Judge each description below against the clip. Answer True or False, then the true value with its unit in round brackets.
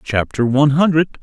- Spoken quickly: False (145 wpm)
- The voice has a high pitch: False (140 Hz)